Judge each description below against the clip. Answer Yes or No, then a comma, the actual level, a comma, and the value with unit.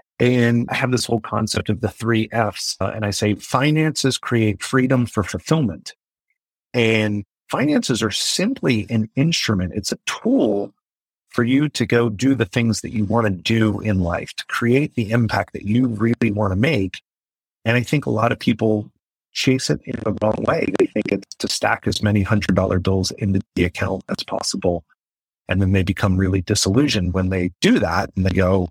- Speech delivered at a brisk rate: No, average, 195 wpm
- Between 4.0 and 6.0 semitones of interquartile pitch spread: No, average, 3.5 semitones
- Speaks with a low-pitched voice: Yes, low, 110 Hz